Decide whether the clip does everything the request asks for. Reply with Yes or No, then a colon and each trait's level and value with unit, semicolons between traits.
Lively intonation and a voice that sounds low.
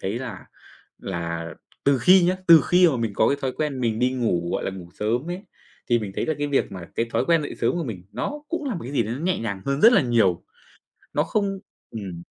Yes: wide, 8.1 semitones; low, 125 Hz